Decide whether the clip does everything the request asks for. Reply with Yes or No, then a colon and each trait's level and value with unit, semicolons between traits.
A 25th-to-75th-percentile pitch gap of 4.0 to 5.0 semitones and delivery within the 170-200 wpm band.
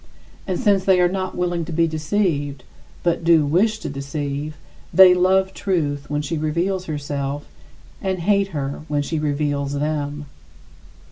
No: average, 4.3 semitones; average, 150 wpm